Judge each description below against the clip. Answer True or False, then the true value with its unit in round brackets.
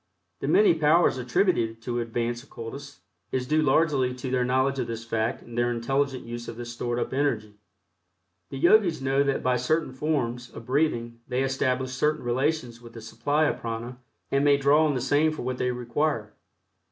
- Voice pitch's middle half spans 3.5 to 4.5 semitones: False (3.1 semitones)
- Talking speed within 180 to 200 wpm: True (190 wpm)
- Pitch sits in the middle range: False (130 Hz)